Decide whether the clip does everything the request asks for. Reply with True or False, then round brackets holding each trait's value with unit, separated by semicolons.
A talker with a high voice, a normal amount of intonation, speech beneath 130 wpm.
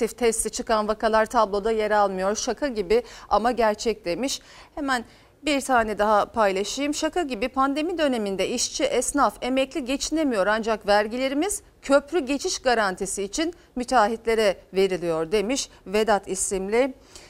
True (230 Hz; 4.7 semitones; 120 wpm)